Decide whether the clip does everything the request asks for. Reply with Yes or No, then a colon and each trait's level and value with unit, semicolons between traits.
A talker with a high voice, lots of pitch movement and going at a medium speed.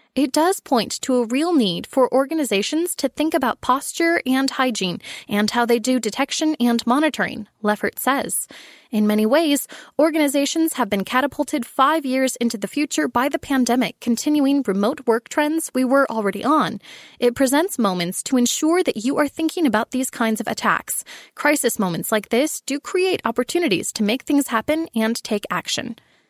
No: very high, 260 Hz; average, 4.5 semitones; average, 170 wpm